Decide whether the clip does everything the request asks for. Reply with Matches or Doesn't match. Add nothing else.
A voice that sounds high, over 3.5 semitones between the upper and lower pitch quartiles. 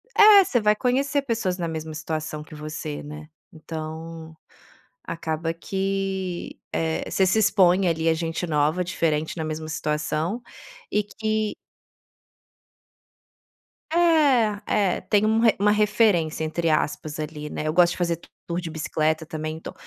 Doesn't match